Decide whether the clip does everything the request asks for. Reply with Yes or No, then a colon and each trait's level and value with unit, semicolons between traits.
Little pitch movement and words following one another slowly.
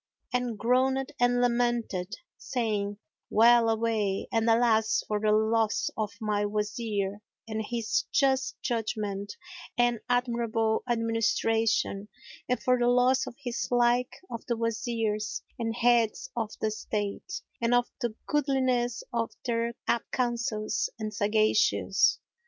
Yes: narrow, 2.1 semitones; slow, 125 wpm